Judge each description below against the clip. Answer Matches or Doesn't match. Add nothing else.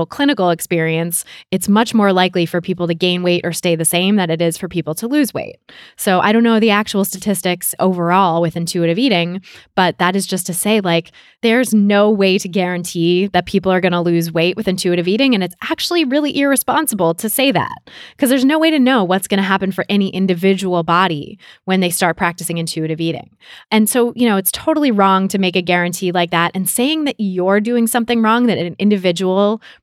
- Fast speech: Matches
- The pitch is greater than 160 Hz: Matches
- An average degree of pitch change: Matches